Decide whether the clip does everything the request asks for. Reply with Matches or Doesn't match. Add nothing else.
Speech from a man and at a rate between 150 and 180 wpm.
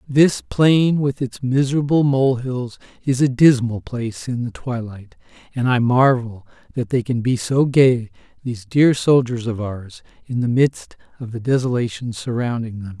Matches